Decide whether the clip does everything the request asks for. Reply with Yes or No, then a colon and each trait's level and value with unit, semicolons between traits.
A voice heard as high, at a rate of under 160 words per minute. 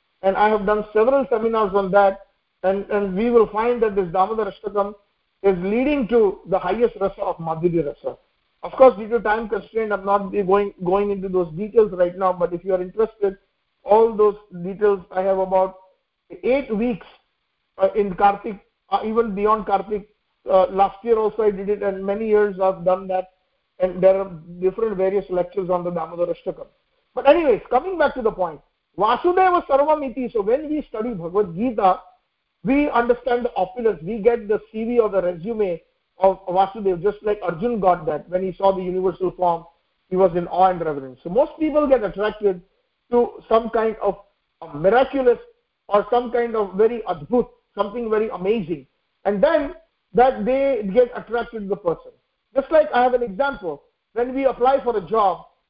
No: high, 210 Hz; average, 180 wpm